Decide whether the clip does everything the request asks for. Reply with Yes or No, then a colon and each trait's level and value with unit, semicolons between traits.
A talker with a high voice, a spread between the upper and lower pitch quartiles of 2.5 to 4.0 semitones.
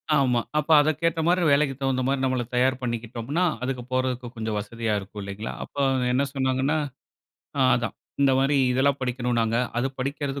No: low, 130 Hz; average, 2.8 semitones